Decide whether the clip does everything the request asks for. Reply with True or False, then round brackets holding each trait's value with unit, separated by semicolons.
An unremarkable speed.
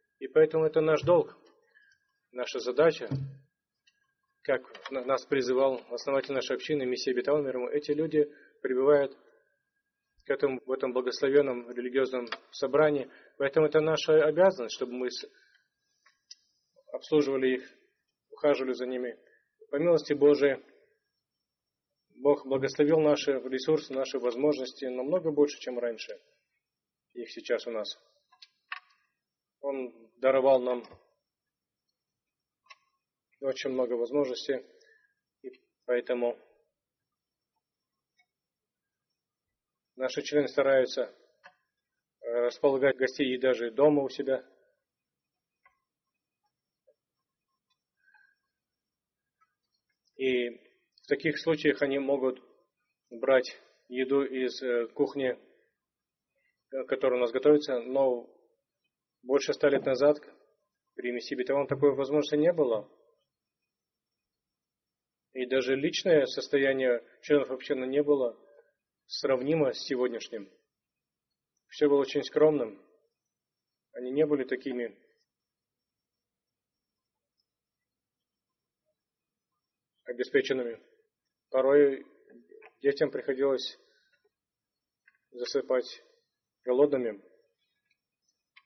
False (85 wpm)